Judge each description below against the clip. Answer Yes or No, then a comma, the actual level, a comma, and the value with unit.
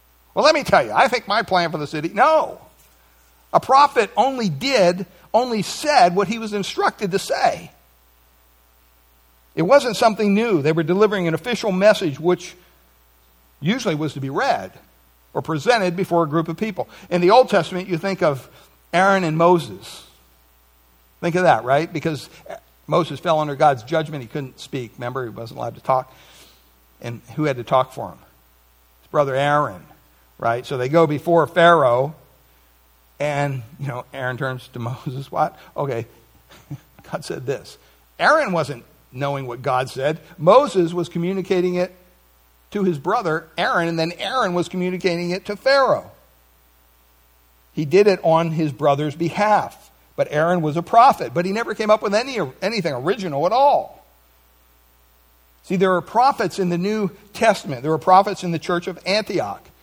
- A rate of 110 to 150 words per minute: No, average, 165 wpm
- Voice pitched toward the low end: No, medium, 155 Hz